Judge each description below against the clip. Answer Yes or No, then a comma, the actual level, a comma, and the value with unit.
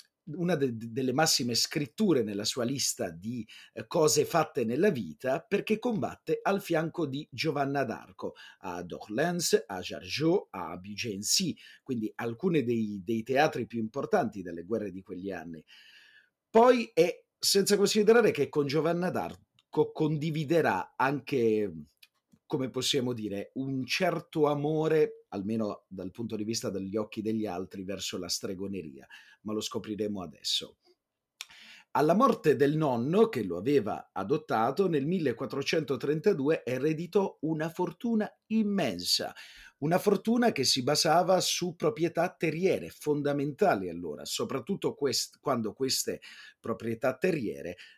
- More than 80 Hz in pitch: Yes, medium, 140 Hz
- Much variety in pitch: Yes, wide, 7.3 semitones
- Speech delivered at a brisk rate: No, average, 125 wpm